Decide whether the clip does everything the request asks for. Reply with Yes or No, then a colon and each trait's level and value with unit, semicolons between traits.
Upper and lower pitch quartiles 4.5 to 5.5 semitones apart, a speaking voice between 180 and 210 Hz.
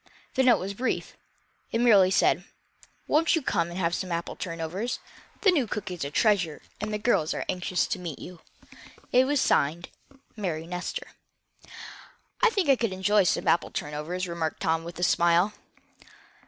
Yes: average, 4.8 semitones; medium, 185 Hz